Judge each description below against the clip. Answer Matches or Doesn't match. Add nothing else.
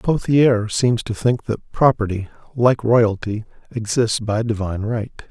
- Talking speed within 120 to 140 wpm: Matches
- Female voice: Doesn't match